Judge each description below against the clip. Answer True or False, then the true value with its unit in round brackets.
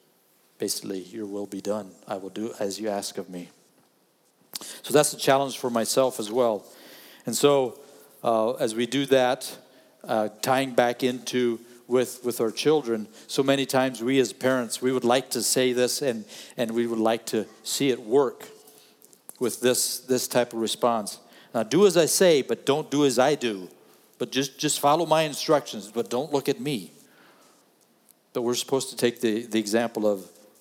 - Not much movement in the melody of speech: False (3.1 semitones)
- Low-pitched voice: True (125 Hz)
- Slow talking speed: False (185 wpm)